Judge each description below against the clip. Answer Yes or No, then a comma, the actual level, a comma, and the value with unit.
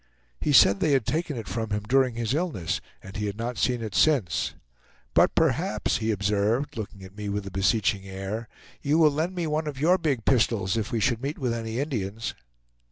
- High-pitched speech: No, low, 115 Hz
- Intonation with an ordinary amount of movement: No, wide, 5.7 semitones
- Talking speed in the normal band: No, fast, 210 wpm